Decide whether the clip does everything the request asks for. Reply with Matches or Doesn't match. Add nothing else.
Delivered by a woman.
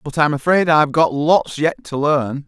Doesn't match